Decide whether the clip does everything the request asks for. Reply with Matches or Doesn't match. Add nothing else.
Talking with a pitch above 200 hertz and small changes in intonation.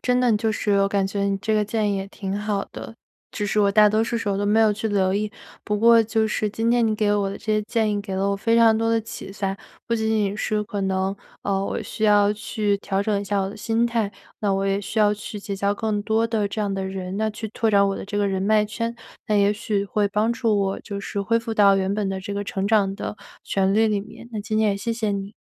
Matches